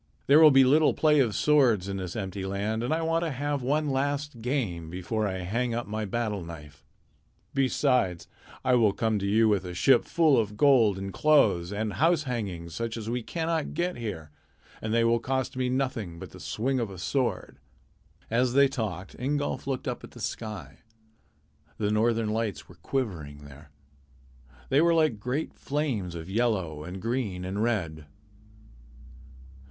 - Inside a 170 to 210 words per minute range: Yes, average, 175 wpm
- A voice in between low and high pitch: No, low, 115 Hz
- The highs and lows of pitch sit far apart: Yes, wide, 5.8 semitones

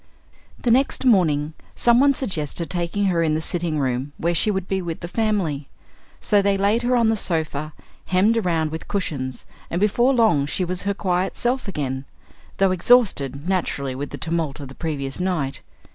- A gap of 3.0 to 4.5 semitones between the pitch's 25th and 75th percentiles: No, average, 5.3 semitones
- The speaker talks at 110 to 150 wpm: No, average, 185 wpm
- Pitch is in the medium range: Yes, medium, 175 Hz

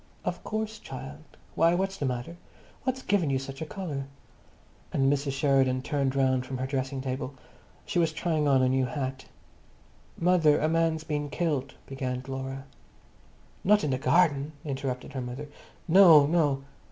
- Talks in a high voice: No, medium, 140 Hz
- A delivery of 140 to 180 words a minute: Yes, average, 160 wpm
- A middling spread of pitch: Yes, average, 3.6 semitones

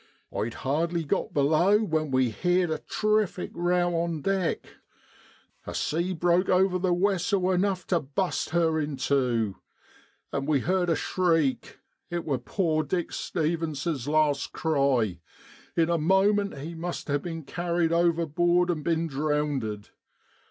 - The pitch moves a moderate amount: Yes, average, 3.5 semitones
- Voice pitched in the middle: Yes, medium, 165 Hz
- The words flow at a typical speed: Yes, average, 150 wpm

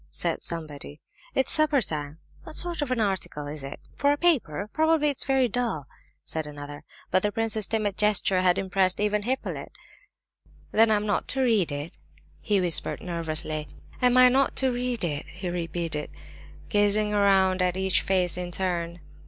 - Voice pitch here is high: Yes, high, 195 Hz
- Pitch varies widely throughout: Yes, wide, 6.2 semitones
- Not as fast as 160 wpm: No, average, 170 wpm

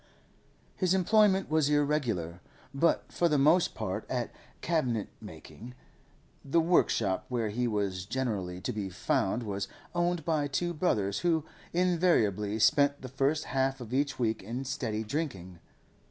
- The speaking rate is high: No, average, 140 wpm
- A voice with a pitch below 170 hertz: Yes, low, 135 Hz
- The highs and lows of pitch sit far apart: Yes, wide, 7.1 semitones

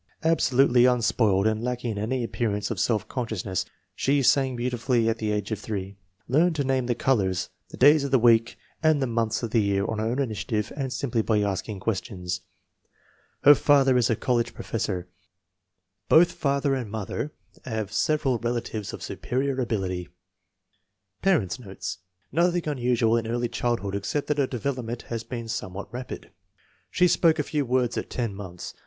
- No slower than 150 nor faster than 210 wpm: Yes, average, 180 wpm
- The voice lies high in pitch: No, low, 120 Hz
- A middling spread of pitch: Yes, average, 3.7 semitones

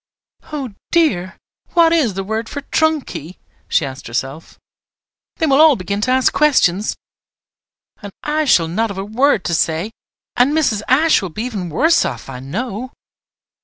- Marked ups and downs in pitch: Yes, wide, 8.3 semitones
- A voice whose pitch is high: Yes, high, 220 Hz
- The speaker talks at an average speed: Yes, average, 165 wpm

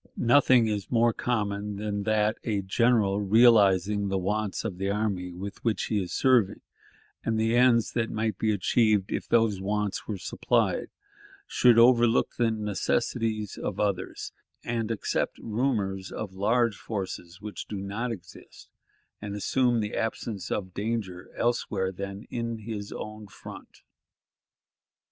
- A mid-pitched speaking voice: No, low, 105 Hz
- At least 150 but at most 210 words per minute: No, average, 140 wpm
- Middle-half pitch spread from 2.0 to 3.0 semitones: Yes, average, 2.7 semitones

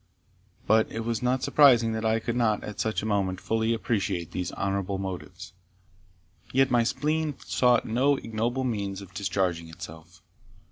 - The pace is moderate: Yes, average, 155 wpm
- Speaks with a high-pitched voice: No, low, 110 Hz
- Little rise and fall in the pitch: No, average, 4.0 semitones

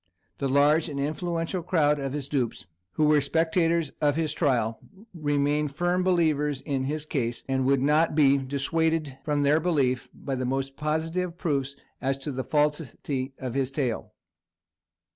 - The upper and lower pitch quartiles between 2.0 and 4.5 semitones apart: Yes, average, 2.8 semitones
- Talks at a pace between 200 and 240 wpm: No, average, 160 wpm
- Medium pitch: Yes, medium, 145 Hz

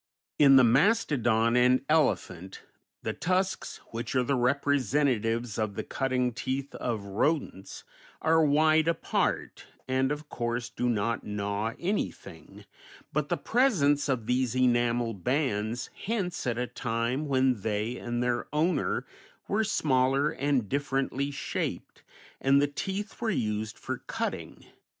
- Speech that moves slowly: Yes, slow, 130 wpm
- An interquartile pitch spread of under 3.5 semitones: No, average, 3.9 semitones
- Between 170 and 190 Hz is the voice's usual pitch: No, low, 130 Hz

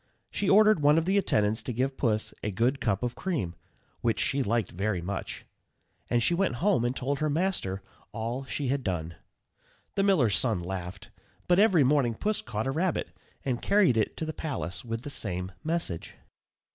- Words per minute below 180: No, average, 185 wpm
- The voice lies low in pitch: Yes, low, 125 Hz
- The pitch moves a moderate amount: No, wide, 7.3 semitones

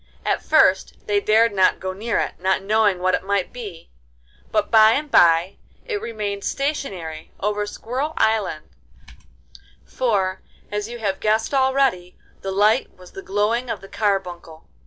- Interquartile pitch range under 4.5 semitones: Yes, average, 3.6 semitones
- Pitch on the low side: No, high, 205 Hz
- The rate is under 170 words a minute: Yes, average, 155 wpm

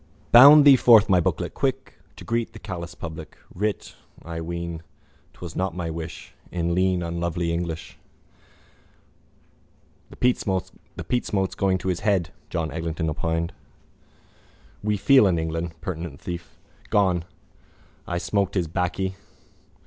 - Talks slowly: Yes, slow, 130 wpm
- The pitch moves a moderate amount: Yes, average, 3.1 semitones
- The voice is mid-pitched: No, very low, 90 Hz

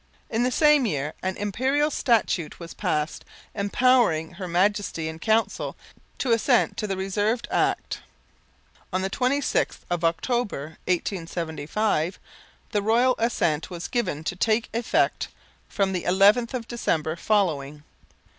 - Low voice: No, high, 200 Hz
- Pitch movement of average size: No, wide, 5.7 semitones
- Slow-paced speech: Yes, slow, 130 wpm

